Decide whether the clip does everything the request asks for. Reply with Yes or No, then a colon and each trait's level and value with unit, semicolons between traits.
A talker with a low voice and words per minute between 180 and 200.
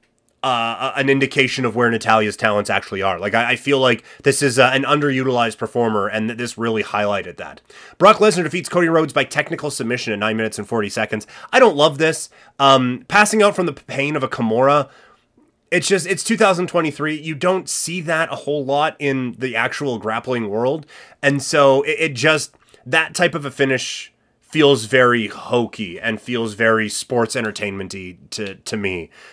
Yes: low, 130 Hz; average, 185 wpm